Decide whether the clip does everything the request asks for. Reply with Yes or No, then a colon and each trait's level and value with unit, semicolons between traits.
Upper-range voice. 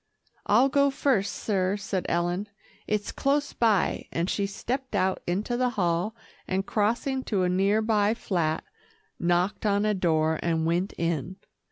Yes: high, 200 Hz